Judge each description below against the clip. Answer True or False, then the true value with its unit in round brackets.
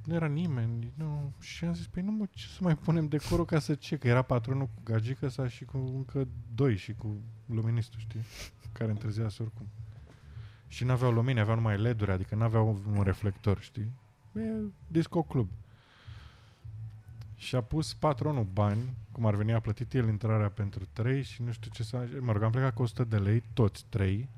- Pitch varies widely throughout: False (3.5 semitones)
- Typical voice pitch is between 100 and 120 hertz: True (115 Hz)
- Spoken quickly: True (195 wpm)